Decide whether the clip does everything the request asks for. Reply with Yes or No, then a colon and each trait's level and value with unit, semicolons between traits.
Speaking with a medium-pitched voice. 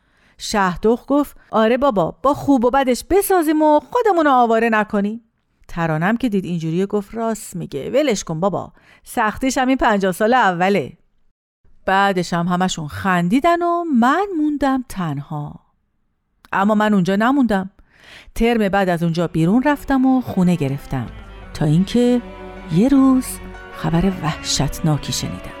No: high, 205 Hz